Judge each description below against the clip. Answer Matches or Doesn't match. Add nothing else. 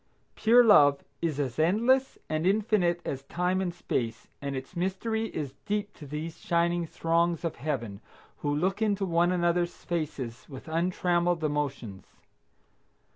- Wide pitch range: Doesn't match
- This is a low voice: Doesn't match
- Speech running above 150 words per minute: Doesn't match